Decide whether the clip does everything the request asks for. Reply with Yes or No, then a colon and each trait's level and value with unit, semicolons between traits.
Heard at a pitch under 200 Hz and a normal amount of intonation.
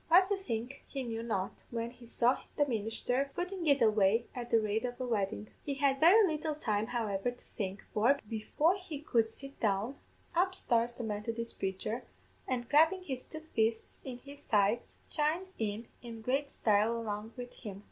No: high, 240 Hz; average, 4.4 semitones